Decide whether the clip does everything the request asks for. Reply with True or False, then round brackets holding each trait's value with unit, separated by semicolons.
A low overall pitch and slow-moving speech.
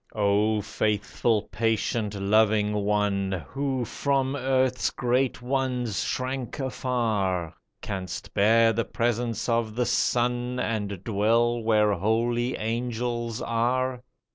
True (115 Hz; 105 wpm)